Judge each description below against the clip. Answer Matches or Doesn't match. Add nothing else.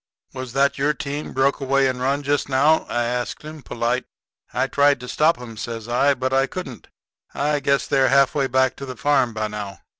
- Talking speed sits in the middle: Doesn't match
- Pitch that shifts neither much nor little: Doesn't match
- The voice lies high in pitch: Doesn't match